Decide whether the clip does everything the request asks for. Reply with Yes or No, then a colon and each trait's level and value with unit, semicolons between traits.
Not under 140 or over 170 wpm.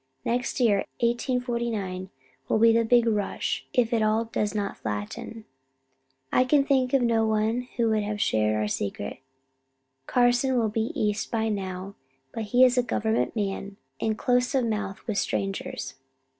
Yes: average, 160 wpm